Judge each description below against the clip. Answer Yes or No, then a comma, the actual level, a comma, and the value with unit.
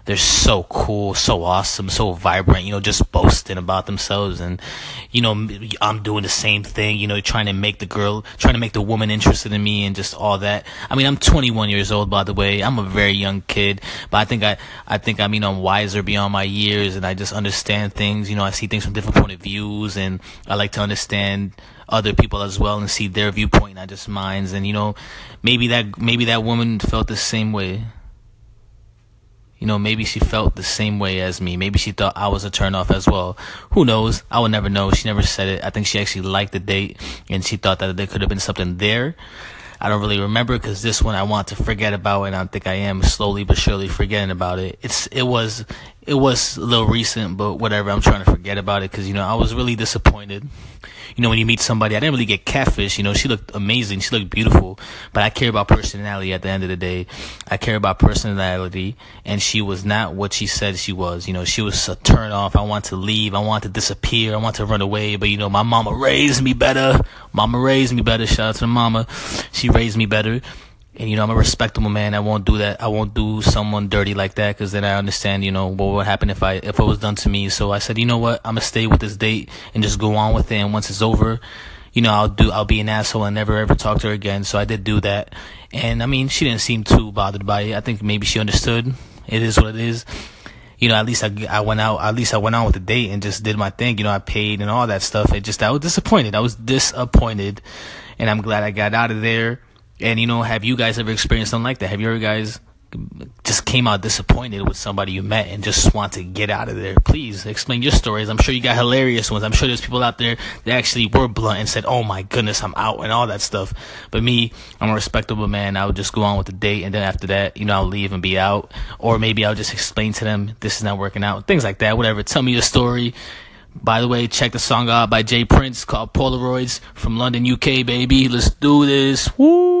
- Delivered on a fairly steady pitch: Yes, narrow, 2.2 semitones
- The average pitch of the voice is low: Yes, low, 105 Hz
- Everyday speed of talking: No, fast, 255 wpm